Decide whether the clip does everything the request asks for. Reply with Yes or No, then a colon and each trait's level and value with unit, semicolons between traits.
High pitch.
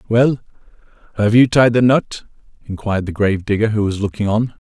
No: low, 110 Hz